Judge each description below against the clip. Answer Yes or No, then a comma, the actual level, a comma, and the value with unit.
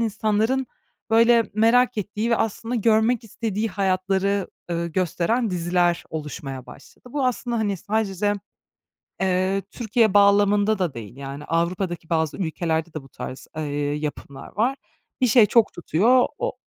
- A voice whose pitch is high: Yes, high, 200 Hz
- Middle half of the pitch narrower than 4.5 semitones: No, average, 4.8 semitones